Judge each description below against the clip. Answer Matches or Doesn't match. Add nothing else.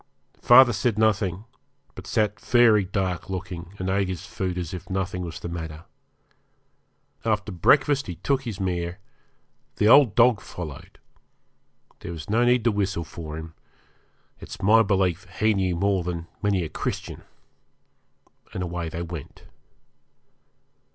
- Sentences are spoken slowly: Doesn't match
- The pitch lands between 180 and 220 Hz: Doesn't match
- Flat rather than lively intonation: Doesn't match